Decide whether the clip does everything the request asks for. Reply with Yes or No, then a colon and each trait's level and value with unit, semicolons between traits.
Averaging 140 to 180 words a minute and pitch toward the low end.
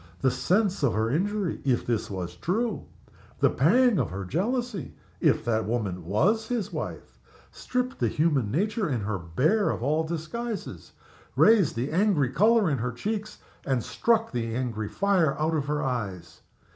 No: average, 165 wpm; medium, 150 Hz